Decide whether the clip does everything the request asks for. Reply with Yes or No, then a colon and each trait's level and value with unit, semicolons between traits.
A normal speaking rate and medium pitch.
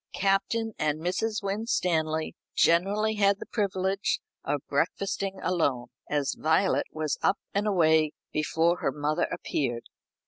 No: slow, 125 wpm; medium, 180 Hz